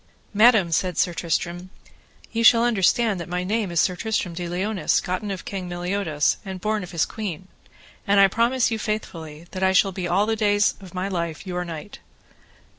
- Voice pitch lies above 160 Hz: Yes, high, 190 Hz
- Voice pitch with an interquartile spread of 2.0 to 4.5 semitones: Yes, average, 3.2 semitones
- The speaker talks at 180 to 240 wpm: Yes, average, 190 wpm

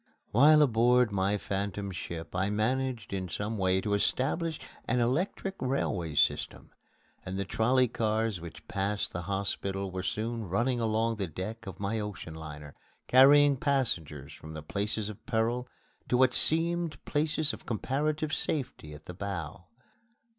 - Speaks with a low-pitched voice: Yes, low, 110 Hz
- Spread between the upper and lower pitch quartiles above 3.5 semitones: Yes, average, 5.3 semitones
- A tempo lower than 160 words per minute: Yes, average, 150 wpm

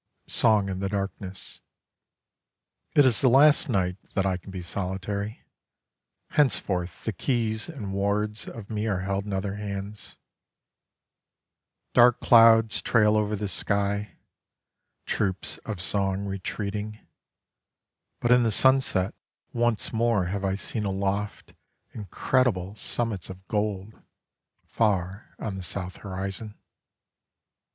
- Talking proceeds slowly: Yes, slow, 120 wpm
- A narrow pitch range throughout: Yes, narrow, 2.3 semitones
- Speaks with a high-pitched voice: No, low, 100 Hz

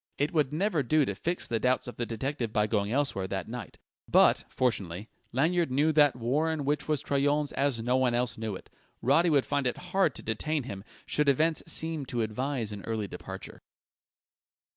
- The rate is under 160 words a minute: No, average, 190 wpm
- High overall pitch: No, low, 135 Hz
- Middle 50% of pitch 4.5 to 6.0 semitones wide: Yes, average, 4.8 semitones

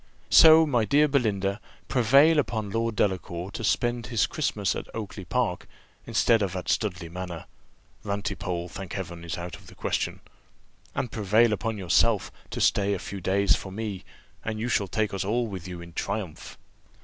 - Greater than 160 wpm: Yes, average, 175 wpm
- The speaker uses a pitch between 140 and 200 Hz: No, low, 100 Hz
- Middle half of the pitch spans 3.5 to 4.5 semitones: Yes, average, 3.8 semitones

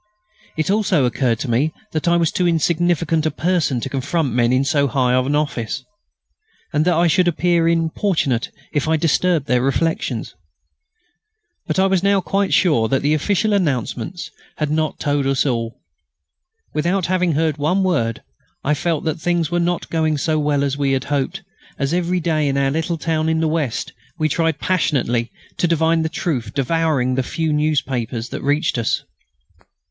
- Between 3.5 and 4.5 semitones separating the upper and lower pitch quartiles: Yes, average, 3.9 semitones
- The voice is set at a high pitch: No, medium, 155 Hz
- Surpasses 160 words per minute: Yes, average, 175 wpm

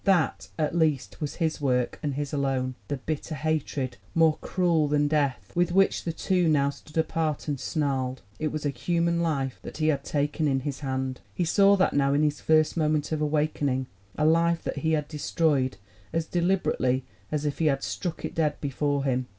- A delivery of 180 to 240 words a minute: Yes, average, 200 wpm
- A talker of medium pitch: Yes, medium, 150 Hz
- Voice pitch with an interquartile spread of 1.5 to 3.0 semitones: Yes, average, 2.7 semitones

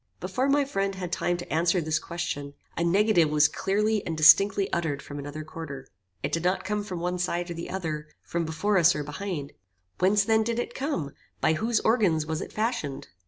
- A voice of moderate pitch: Yes, medium, 175 Hz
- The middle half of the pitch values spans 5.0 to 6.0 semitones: No, average, 4.6 semitones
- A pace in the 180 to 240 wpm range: Yes, fast, 205 wpm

